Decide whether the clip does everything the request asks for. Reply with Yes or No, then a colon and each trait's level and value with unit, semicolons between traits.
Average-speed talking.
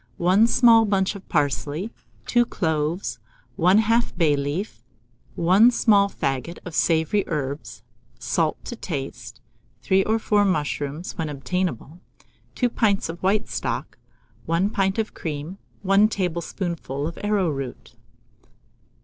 No: slow, 120 wpm